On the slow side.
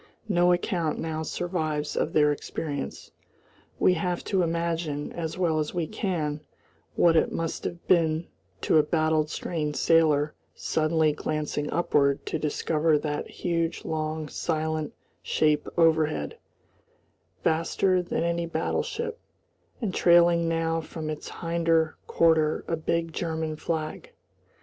Yes: slow, 125 wpm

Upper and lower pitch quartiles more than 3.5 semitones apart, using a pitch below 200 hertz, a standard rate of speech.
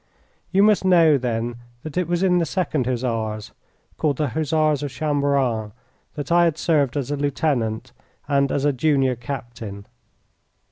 Yes: average, 4.6 semitones; medium, 140 Hz; average, 155 wpm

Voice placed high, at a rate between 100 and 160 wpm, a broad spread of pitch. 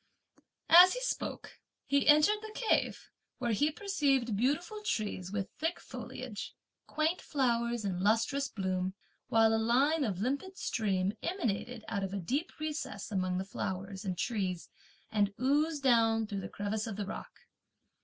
Yes: high, 230 Hz; average, 155 wpm; wide, 6.6 semitones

